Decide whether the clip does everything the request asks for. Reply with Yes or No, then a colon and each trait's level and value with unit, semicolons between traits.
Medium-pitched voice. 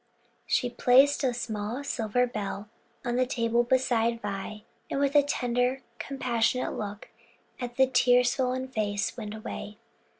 No: high, 245 Hz